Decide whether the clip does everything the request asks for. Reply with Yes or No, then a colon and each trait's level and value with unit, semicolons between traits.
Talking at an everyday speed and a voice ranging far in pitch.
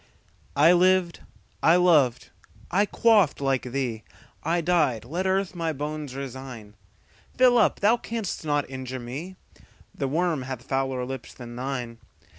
No: slow, 125 wpm; wide, 5.7 semitones